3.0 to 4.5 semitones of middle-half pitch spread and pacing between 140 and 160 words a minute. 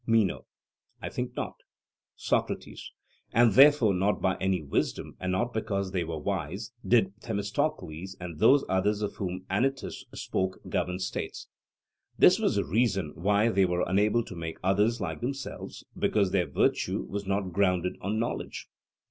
Yes: average, 3.3 semitones; average, 155 wpm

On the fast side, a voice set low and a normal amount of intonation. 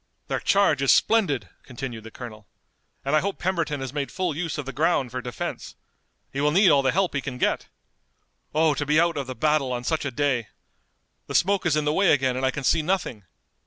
No: fast, 230 wpm; medium, 145 Hz; average, 4.0 semitones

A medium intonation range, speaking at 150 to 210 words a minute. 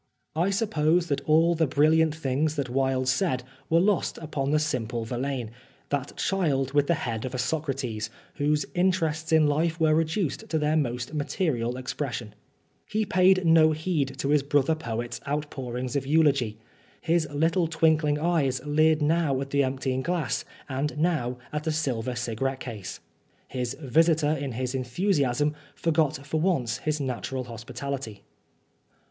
Yes: average, 3.7 semitones; average, 160 wpm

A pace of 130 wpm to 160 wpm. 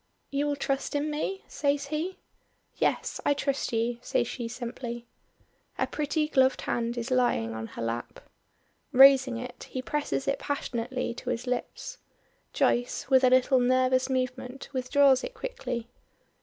Yes: average, 150 wpm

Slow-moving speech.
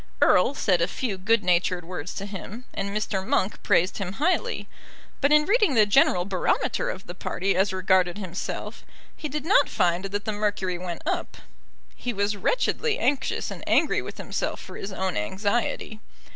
No: average, 175 wpm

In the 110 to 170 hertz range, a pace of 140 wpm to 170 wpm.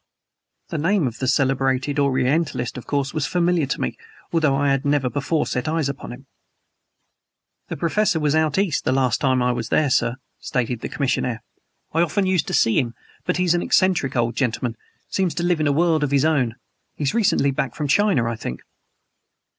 No: medium, 140 Hz; average, 195 wpm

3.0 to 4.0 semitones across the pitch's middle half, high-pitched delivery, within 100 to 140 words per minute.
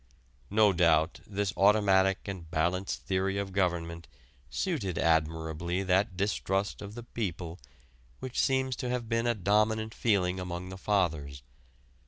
No: average, 3.4 semitones; very low, 95 Hz; slow, 135 wpm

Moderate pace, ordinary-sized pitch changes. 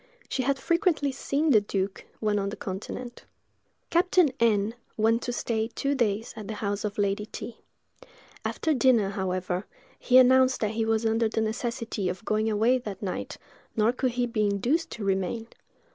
Yes: average, 175 wpm; average, 3.6 semitones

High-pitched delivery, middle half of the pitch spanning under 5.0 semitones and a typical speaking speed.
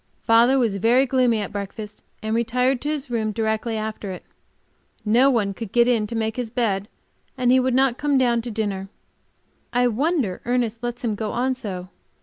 Yes: high, 235 Hz; average, 2.7 semitones; average, 190 wpm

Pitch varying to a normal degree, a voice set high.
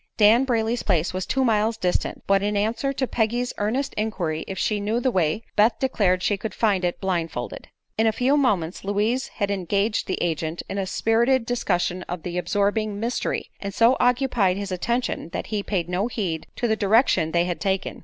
Yes: average, 4.0 semitones; high, 205 Hz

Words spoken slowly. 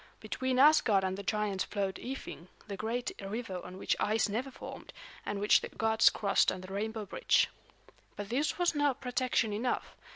No: average, 175 wpm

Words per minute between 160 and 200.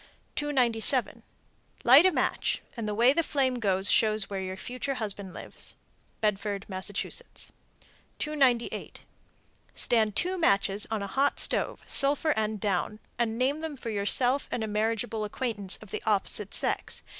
No: average, 150 wpm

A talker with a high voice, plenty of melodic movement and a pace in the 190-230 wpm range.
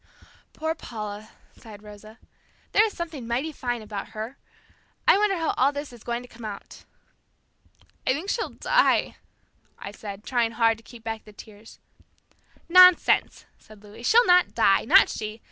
No: high, 235 Hz; wide, 6.7 semitones; average, 160 wpm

